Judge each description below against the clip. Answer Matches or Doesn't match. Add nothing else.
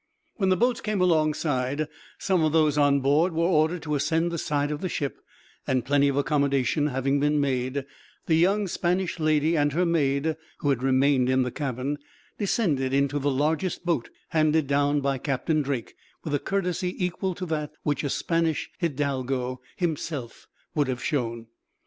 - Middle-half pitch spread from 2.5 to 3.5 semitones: Matches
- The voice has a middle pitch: Matches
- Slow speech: Doesn't match